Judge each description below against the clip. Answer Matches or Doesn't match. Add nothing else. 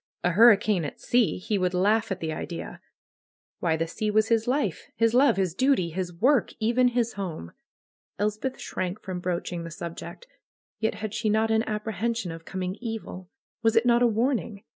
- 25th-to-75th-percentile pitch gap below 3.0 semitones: Doesn't match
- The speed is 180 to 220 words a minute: Matches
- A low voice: Doesn't match